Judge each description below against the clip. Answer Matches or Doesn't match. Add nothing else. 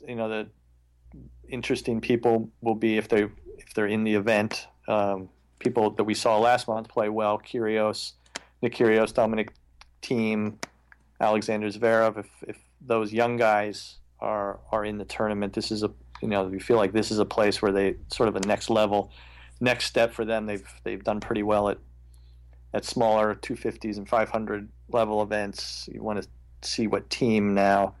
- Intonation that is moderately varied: Doesn't match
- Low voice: Matches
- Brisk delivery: Doesn't match